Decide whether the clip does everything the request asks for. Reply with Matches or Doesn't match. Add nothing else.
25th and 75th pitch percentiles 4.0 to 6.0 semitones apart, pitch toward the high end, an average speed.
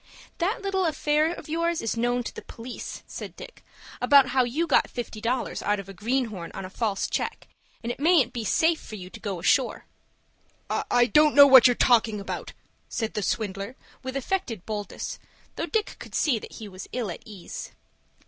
Matches